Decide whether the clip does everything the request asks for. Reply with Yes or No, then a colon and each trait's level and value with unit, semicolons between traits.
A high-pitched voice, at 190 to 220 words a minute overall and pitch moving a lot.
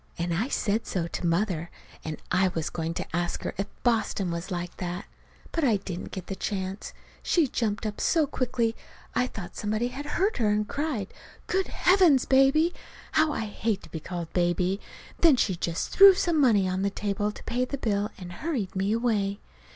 Yes: high, 210 Hz; average, 195 wpm; wide, 5.9 semitones